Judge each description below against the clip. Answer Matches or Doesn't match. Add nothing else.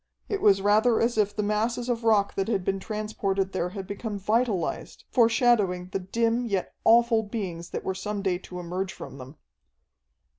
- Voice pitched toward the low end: Doesn't match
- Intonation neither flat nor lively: Matches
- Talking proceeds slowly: Doesn't match